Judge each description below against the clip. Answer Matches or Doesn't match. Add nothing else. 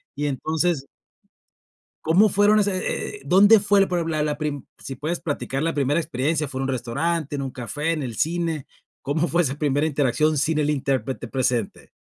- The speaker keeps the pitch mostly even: Doesn't match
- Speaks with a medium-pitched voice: Matches